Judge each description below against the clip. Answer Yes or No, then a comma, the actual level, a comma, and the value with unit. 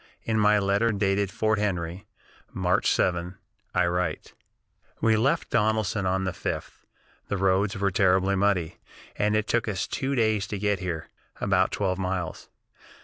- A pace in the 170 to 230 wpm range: No, average, 150 wpm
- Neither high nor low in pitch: No, low, 100 Hz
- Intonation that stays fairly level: Yes, narrow, 2.3 semitones